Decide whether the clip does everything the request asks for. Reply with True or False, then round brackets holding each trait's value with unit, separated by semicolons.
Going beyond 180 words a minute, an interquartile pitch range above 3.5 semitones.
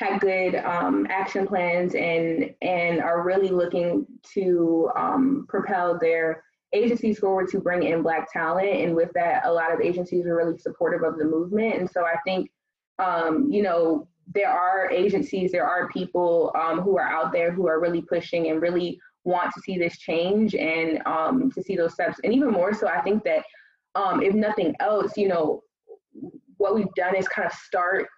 False (190 wpm; 3.1 semitones)